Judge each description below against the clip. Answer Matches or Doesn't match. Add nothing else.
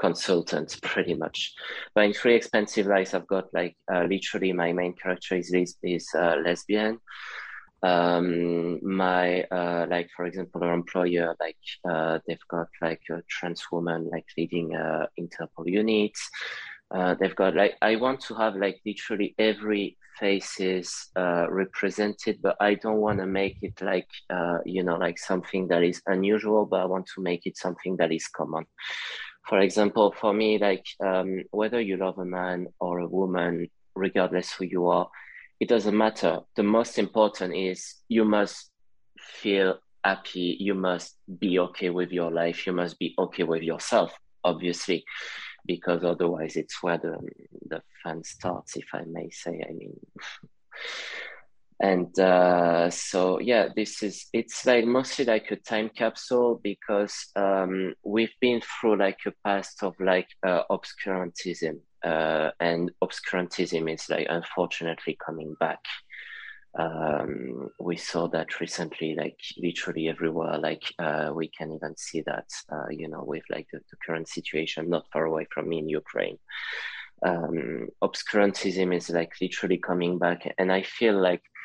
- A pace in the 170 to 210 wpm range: Doesn't match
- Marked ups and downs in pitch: Doesn't match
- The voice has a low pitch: Matches